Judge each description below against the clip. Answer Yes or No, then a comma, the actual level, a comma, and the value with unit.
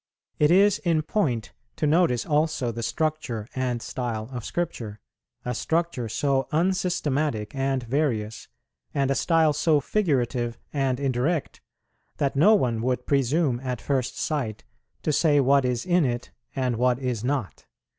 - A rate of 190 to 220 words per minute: No, average, 145 wpm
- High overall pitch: No, low, 135 Hz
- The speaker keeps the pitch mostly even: No, average, 4.2 semitones